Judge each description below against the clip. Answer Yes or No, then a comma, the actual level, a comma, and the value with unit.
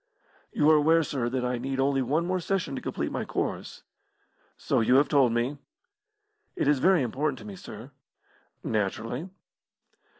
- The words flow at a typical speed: Yes, average, 165 wpm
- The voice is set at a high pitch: No, low, 135 Hz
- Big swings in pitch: No, average, 3.9 semitones